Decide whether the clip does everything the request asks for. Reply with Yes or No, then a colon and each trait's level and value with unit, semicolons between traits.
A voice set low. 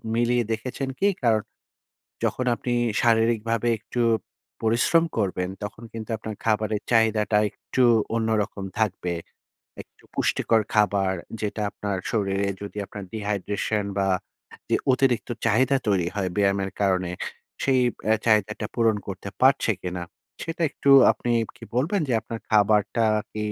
Yes: low, 110 Hz